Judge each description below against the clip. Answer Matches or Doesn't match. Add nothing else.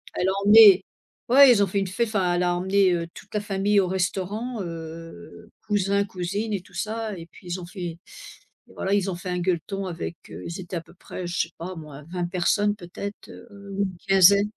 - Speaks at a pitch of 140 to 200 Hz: Matches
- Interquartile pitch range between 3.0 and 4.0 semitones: Doesn't match